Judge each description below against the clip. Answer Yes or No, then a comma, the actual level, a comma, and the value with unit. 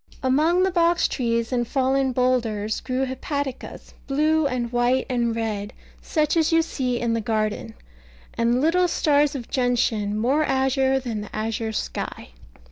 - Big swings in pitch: No, average, 3.8 semitones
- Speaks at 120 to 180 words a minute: Yes, average, 150 wpm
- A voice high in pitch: Yes, very high, 255 Hz